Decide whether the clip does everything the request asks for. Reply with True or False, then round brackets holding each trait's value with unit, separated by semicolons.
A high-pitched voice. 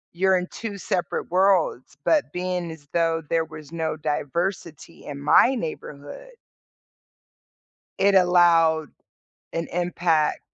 False (170 Hz)